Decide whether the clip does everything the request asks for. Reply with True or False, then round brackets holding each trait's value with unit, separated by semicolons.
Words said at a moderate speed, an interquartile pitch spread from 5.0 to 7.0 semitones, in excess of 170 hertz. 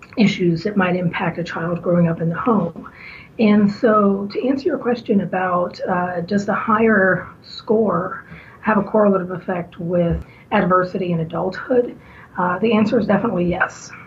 False (160 wpm; 3.3 semitones; 190 Hz)